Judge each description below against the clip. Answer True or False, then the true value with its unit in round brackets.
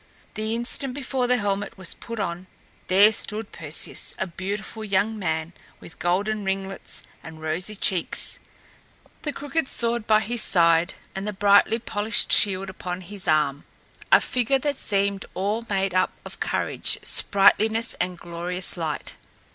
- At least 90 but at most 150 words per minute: True (145 wpm)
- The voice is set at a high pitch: True (200 Hz)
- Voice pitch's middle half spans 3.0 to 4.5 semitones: True (3.5 semitones)